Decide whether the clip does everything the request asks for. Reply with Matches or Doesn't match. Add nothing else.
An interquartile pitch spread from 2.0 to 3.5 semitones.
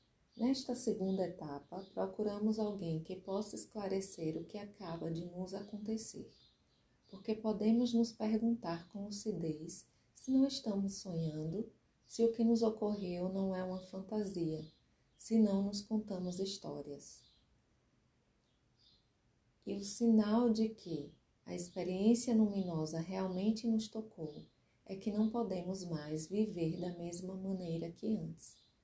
Doesn't match